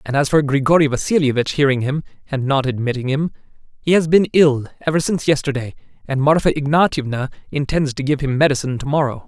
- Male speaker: Yes, male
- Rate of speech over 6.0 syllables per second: Yes, 6.3 syllables/s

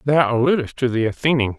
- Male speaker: Yes, male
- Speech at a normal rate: Yes, average, 190 wpm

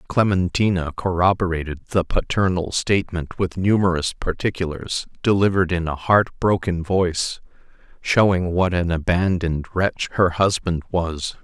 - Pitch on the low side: Yes, very low, 90 Hz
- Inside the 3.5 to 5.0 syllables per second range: Yes, 4.7 syllables/s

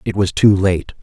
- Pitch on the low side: Yes, very low, 95 Hz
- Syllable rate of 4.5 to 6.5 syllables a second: Yes, 4.8 syllables/s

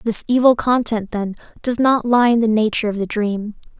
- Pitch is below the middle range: No, high, 225 Hz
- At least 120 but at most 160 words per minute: No, fast, 205 wpm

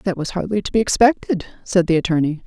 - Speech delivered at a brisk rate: Yes, fast, 220 wpm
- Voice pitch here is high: No, medium, 180 Hz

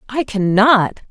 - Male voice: No, female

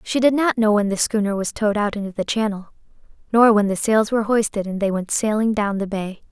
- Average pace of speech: No, fast, 245 wpm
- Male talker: No, female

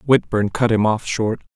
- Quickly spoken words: No, average, 195 wpm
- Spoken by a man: Yes, male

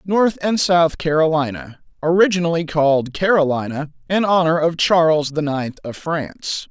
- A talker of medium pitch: Yes, medium, 160 Hz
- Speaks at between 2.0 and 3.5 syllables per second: No, 4.7 syllables/s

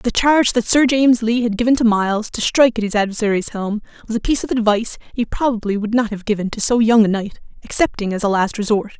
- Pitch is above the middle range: Yes, high, 225 Hz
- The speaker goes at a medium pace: No, fast, 245 wpm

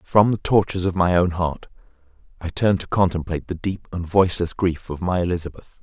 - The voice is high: No, very low, 90 Hz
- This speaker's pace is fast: No, average, 195 wpm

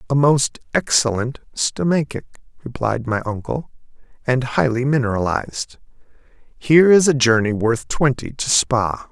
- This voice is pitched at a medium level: No, low, 125 Hz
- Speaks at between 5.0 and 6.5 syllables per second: No, 4.5 syllables/s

